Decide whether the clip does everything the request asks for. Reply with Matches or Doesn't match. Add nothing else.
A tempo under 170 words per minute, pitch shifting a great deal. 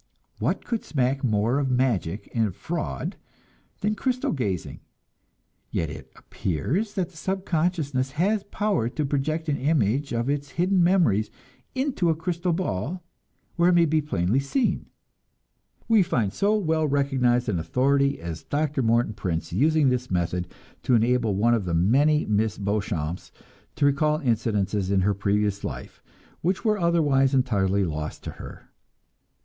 Matches